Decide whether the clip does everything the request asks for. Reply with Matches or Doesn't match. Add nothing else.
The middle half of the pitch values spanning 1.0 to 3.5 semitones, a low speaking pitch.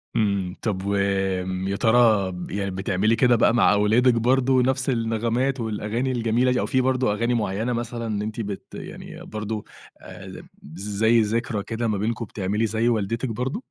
Matches